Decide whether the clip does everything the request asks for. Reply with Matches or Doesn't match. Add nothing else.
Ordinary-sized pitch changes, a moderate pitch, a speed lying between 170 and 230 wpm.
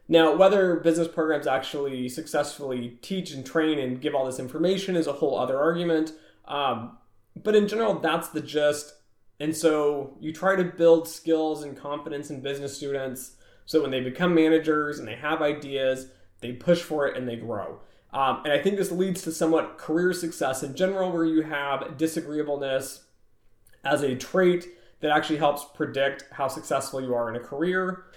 Matches